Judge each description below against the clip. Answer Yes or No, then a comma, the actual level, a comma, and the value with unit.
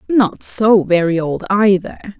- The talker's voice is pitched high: Yes, high, 195 Hz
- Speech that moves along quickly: No, slow, 135 wpm